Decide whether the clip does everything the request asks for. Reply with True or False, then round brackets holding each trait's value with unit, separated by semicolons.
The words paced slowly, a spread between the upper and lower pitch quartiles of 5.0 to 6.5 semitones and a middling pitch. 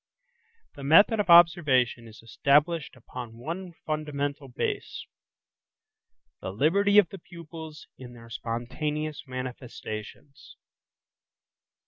True (90 wpm; 5.3 semitones; 145 Hz)